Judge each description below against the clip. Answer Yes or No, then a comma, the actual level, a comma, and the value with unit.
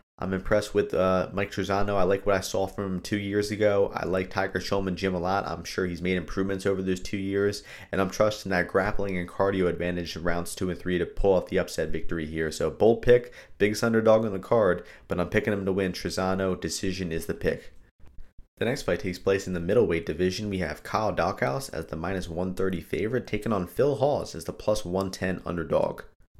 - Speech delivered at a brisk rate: Yes, fast, 225 wpm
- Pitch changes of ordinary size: No, narrow, 2.0 semitones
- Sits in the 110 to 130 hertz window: No, very low, 95 Hz